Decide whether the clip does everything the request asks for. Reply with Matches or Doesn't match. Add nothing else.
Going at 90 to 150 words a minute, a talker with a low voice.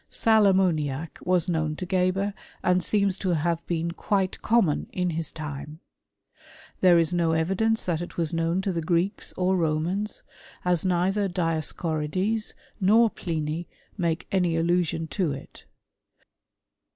Doesn't match